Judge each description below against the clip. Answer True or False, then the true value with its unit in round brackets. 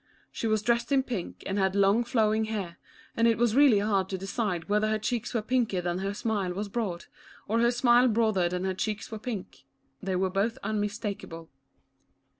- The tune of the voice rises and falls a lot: False (3.2 semitones)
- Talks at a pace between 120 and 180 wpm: False (200 wpm)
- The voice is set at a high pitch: True (210 Hz)